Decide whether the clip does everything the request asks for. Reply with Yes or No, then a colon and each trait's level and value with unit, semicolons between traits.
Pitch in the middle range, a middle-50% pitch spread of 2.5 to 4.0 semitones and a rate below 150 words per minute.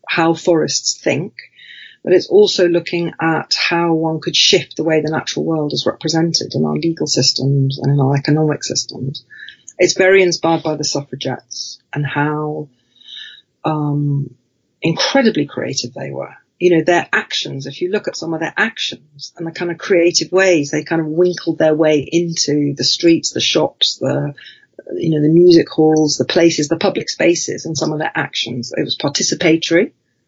No: medium, 160 Hz; average, 2.8 semitones; average, 175 wpm